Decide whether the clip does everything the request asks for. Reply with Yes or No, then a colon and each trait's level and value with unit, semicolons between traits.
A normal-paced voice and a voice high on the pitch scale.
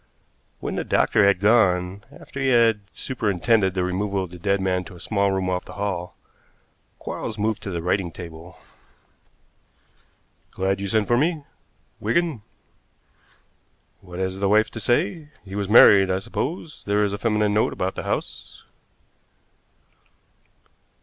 No: average, 150 wpm; low, 100 Hz